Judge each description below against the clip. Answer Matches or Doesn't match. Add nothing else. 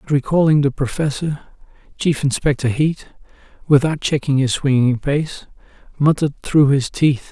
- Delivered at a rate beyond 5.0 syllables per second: Doesn't match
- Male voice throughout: Matches